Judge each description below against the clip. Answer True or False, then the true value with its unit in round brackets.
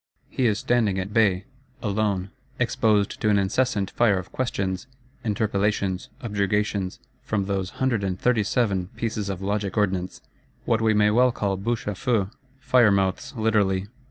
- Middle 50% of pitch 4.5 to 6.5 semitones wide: False (2.5 semitones)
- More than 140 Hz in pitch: False (105 Hz)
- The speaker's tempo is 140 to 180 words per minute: True (150 wpm)